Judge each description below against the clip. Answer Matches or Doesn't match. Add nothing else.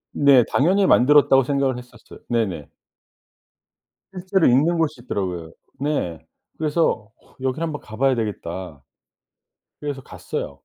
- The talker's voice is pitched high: Doesn't match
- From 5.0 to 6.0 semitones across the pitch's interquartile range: Matches